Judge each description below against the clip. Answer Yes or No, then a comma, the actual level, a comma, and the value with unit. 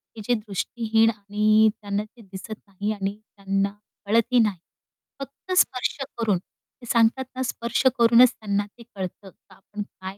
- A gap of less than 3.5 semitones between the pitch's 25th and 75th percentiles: Yes, average, 2.7 semitones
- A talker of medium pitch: No, high, 215 Hz